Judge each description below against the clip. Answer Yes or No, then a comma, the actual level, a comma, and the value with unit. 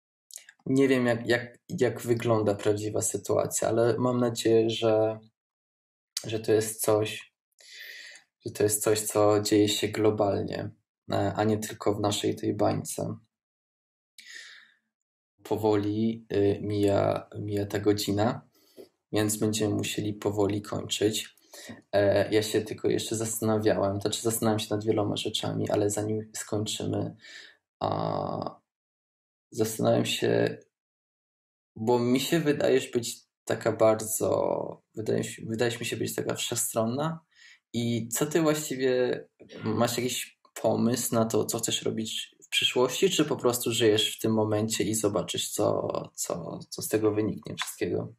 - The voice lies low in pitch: Yes, low, 110 Hz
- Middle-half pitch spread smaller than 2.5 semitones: Yes, narrow, 2.0 semitones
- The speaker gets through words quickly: No, average, 130 wpm